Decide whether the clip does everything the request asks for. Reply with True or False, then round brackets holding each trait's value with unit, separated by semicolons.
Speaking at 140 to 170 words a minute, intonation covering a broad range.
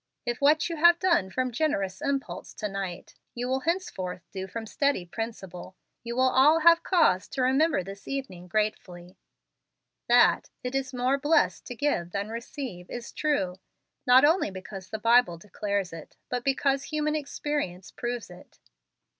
True (160 wpm; 6.7 semitones)